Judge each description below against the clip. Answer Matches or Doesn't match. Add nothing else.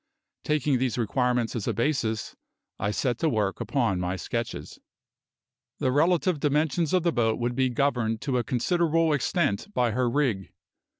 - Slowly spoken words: Doesn't match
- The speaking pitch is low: Matches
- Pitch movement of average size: Matches